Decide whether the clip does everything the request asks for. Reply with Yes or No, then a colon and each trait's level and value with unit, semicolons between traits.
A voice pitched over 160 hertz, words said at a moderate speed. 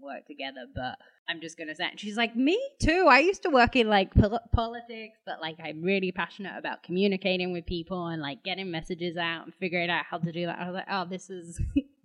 No: medium, 185 Hz; fast, 240 wpm